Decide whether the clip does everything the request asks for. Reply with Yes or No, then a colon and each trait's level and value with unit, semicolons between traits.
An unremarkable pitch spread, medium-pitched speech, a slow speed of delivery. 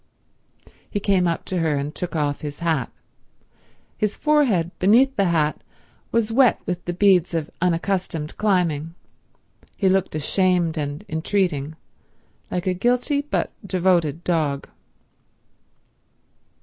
Yes: average, 3.9 semitones; medium, 175 Hz; slow, 125 wpm